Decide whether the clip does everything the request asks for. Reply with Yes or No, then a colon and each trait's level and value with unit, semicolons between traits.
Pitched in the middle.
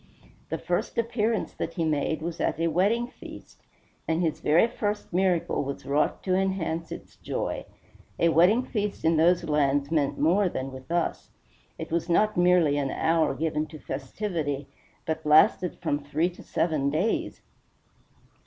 Yes: medium, 165 Hz